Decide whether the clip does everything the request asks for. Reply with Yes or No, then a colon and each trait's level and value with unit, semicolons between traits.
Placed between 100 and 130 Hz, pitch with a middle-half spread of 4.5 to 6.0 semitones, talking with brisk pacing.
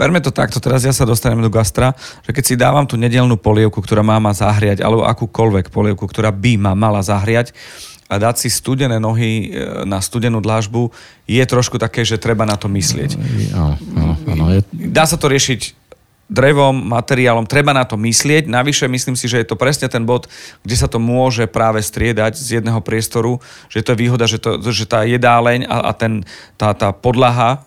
No: low, 115 Hz; narrow, 2.4 semitones; fast, 190 wpm